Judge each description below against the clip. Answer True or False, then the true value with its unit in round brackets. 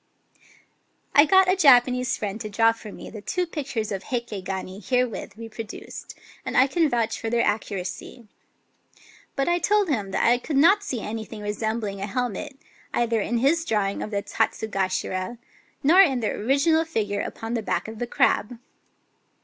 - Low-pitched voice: False (230 Hz)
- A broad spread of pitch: False (4.7 semitones)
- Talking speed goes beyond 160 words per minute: True (175 wpm)